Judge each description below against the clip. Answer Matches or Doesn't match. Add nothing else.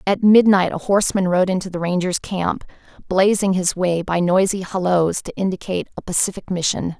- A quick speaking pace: Doesn't match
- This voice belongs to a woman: Matches